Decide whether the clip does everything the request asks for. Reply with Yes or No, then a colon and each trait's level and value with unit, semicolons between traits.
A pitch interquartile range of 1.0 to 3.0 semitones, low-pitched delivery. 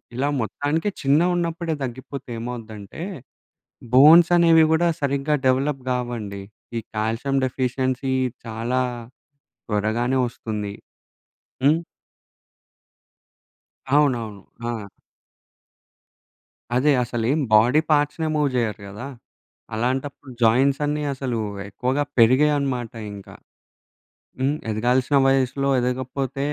No: average, 3.8 semitones; low, 130 Hz